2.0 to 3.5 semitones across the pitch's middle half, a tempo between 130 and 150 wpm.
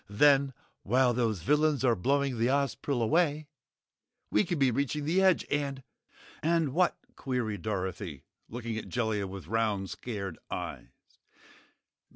No: average, 5.1 semitones; average, 140 wpm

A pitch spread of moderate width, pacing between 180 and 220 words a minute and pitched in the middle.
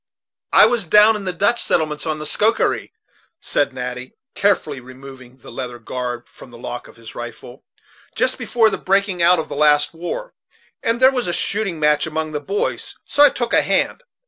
No: wide, 8.2 semitones; average, 195 wpm; medium, 160 Hz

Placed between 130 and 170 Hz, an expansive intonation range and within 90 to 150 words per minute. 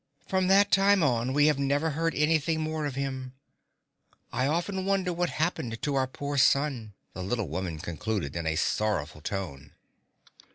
No: medium, 140 Hz; wide, 7.1 semitones; average, 165 wpm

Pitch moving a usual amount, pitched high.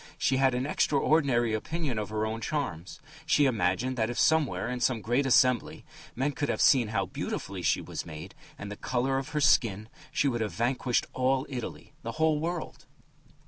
No: average, 4.0 semitones; low, 125 Hz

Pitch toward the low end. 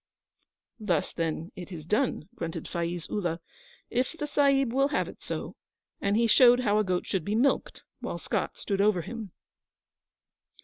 No: high, 210 Hz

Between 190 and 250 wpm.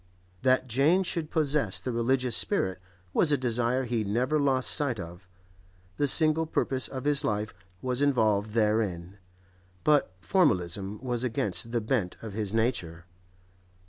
No: average, 145 wpm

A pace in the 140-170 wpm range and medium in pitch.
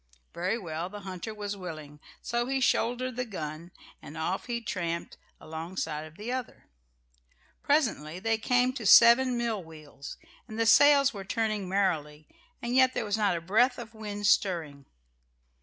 No: average, 160 wpm; high, 205 Hz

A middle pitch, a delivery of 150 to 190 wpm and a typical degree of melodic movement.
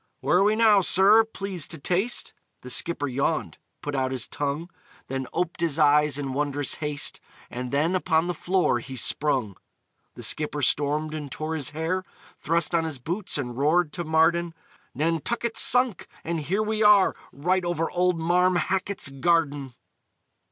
Yes: medium, 160 Hz; average, 165 wpm; average, 3.9 semitones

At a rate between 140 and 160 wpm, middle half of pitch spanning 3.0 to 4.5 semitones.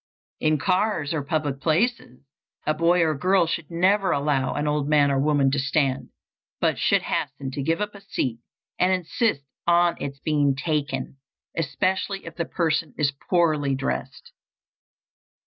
Yes: average, 155 wpm; average, 3.6 semitones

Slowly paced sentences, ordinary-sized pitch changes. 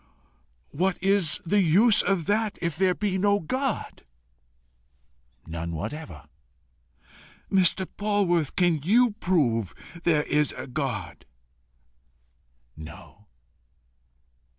No: slow, 95 wpm; wide, 7.1 semitones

